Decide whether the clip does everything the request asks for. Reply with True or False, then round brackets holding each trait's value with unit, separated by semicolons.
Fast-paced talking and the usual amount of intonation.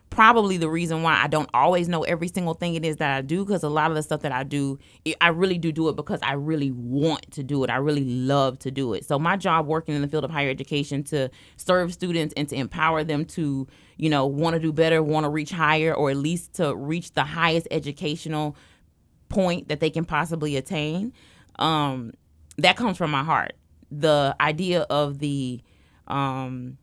True (215 wpm; 3.0 semitones)